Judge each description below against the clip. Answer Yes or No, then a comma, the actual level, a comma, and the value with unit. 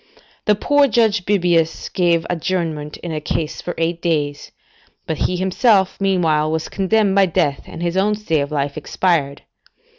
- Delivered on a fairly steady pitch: No, average, 3.8 semitones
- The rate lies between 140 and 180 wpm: Yes, average, 160 wpm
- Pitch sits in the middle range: Yes, medium, 175 Hz